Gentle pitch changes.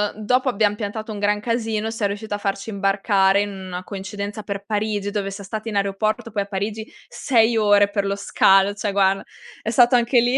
Yes: narrow, 1.7 semitones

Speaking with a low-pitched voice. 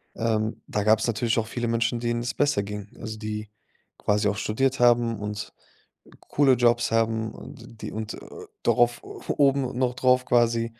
Yes: low, 115 Hz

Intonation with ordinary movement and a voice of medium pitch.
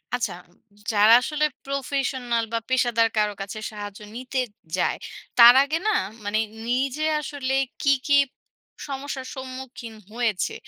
No: average, 3.2 semitones; very high, 250 Hz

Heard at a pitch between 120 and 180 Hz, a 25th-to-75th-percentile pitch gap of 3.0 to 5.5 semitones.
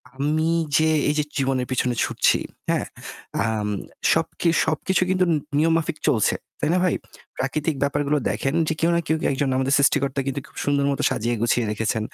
Yes: medium, 140 Hz; average, 3.5 semitones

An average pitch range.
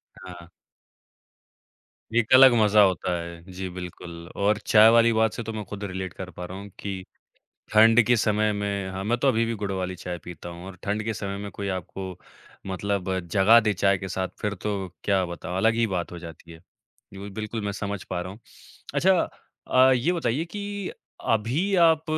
Yes: average, 3.3 semitones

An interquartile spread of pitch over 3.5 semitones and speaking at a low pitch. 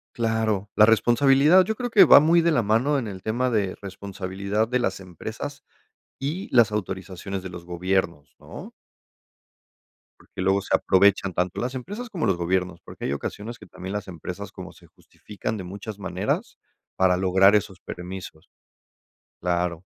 Yes: average, 4.3 semitones; low, 100 Hz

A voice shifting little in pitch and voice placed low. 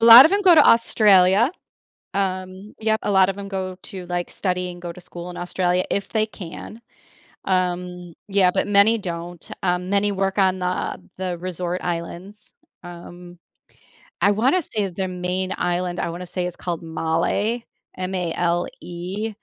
No: narrow, 2.2 semitones; medium, 185 Hz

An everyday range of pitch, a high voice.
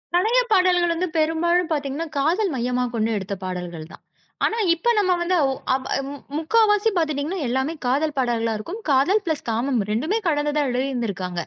No: wide, 6.3 semitones; very high, 295 Hz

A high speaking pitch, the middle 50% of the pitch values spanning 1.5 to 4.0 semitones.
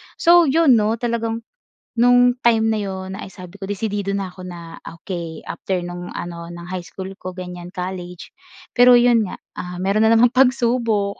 No: high, 200 Hz; average, 4.6 semitones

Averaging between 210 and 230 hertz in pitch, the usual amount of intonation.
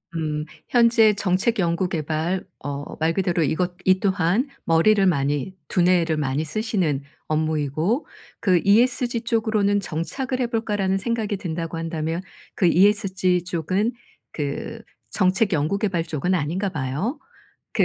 No: medium, 185 Hz; average, 4.6 semitones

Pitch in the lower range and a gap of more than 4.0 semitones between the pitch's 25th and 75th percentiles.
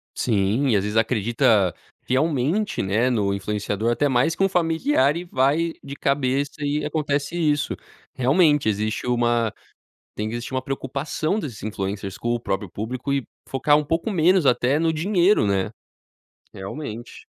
Yes: low, 130 Hz; wide, 5.6 semitones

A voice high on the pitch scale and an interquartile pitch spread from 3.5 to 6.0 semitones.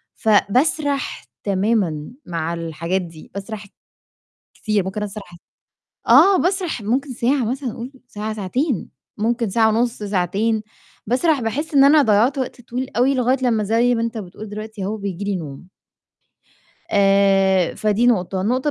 Yes: high, 220 Hz; average, 4.1 semitones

